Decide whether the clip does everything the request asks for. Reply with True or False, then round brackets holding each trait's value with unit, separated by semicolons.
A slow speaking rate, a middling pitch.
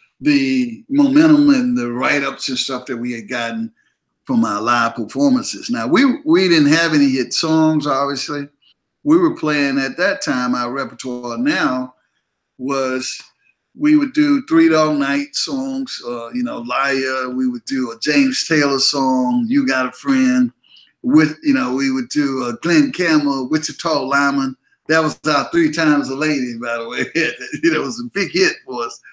False (175 wpm; 150 Hz)